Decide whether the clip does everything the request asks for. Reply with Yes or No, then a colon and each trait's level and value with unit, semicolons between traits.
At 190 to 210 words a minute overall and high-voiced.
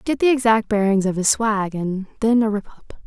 No: fast, 255 wpm; high, 215 Hz